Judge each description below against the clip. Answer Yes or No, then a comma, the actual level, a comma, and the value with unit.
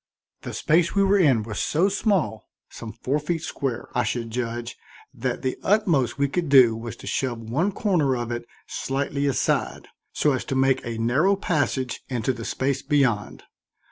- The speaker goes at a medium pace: Yes, average, 175 wpm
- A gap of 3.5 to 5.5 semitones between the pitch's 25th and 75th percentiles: Yes, average, 4.9 semitones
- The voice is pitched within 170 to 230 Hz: No, low, 135 Hz